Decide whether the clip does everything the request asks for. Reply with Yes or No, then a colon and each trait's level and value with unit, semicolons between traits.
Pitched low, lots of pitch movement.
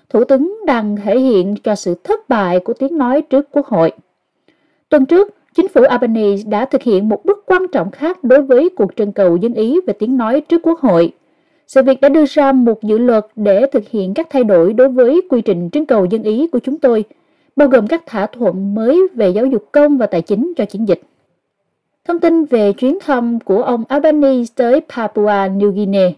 No: very high, 250 Hz; wide, 5.9 semitones